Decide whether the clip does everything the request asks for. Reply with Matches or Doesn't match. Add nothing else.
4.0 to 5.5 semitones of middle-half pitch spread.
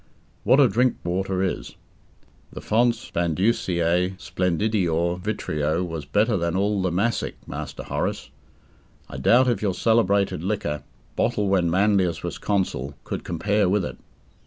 Doesn't match